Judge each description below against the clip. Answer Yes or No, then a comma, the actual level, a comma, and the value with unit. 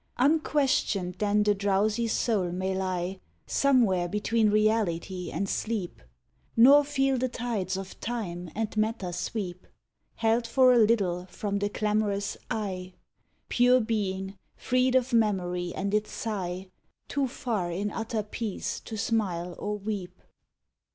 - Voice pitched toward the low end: No, high, 210 Hz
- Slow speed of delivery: Yes, slow, 130 wpm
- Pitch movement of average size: Yes, average, 3.6 semitones